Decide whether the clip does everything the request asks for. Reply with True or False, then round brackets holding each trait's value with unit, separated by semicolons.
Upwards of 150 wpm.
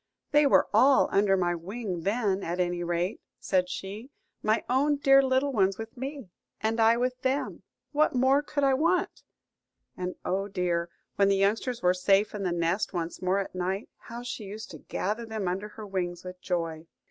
True (190 wpm)